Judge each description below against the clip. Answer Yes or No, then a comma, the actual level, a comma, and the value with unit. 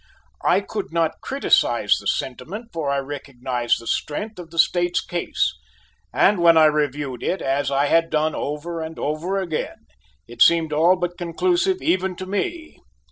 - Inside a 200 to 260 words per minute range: No, average, 165 wpm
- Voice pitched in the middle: Yes, medium, 165 Hz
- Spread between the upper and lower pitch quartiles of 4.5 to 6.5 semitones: No, average, 4.1 semitones